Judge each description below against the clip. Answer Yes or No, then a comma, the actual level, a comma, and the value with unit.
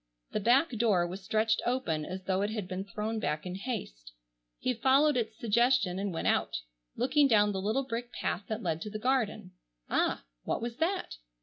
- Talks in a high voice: Yes, high, 215 Hz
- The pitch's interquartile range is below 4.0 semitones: No, average, 4.4 semitones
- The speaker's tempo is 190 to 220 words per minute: Yes, average, 195 wpm